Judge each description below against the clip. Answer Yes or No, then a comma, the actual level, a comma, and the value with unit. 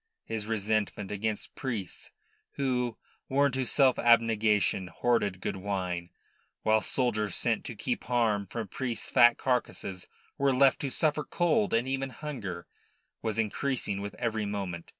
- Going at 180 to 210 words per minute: No, average, 140 wpm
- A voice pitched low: Yes, low, 115 Hz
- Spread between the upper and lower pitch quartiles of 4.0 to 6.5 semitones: Yes, average, 4.3 semitones